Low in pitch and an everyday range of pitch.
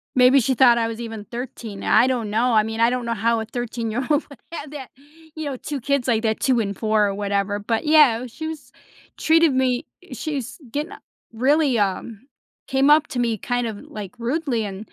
No: high, 240 Hz; average, 3.6 semitones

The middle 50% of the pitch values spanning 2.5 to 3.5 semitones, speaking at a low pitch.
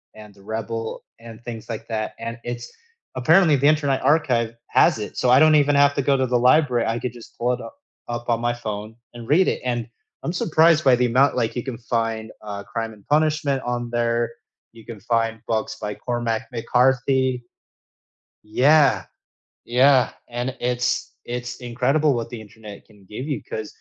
Yes: average, 2.9 semitones; low, 120 Hz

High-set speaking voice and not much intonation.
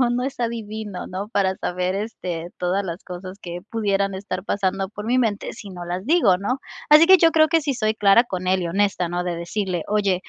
No: high, 200 Hz; average, 3.7 semitones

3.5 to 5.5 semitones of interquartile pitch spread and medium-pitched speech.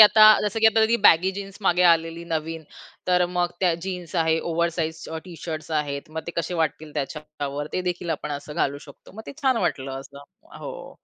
No: average, 3.0 semitones; medium, 165 Hz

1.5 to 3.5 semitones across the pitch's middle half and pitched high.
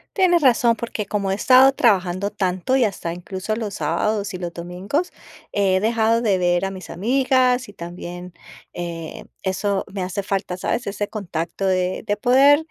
No: average, 4.2 semitones; high, 200 Hz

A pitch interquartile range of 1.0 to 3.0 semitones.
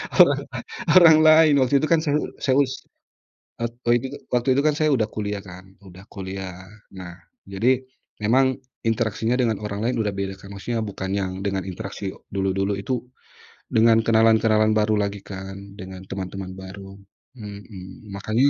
No: average, 3.5 semitones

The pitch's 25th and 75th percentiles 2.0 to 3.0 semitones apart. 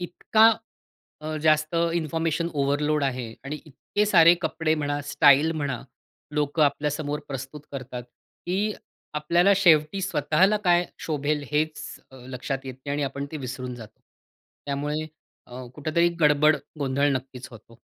Yes: narrow, 2.6 semitones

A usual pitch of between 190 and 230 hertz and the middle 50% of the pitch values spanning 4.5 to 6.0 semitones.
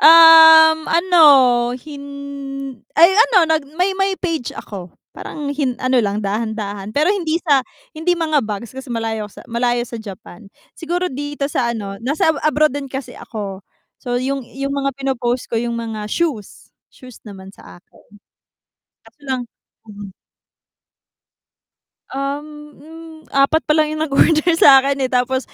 No: very high, 275 Hz; average, 5.2 semitones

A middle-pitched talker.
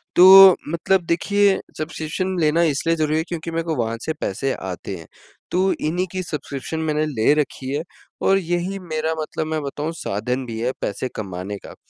Yes: medium, 155 Hz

